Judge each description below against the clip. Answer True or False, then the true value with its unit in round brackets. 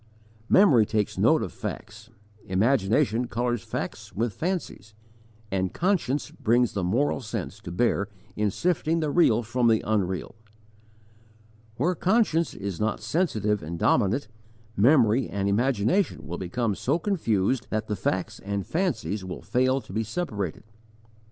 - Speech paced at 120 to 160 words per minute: True (135 wpm)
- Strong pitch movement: True (5.8 semitones)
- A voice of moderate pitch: False (115 Hz)